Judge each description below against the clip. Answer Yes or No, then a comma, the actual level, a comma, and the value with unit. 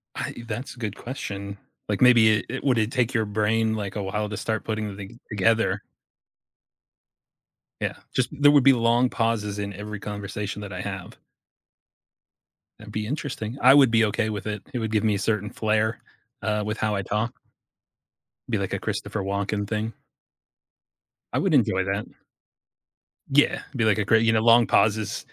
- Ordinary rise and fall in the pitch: No, narrow, 2.0 semitones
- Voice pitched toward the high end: No, low, 110 Hz